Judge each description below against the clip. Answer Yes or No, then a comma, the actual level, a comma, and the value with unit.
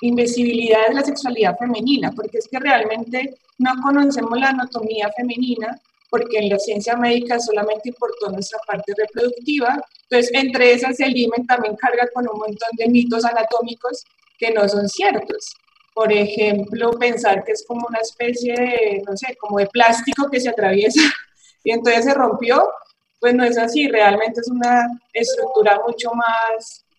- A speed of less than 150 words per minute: No, average, 160 wpm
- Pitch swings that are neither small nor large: No, narrow, 2.3 semitones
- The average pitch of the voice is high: Yes, high, 235 Hz